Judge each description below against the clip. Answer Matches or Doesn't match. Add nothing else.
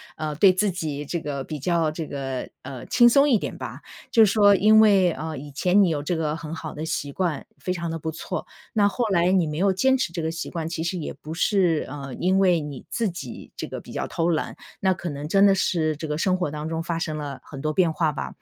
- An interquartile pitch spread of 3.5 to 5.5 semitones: Matches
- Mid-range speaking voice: Matches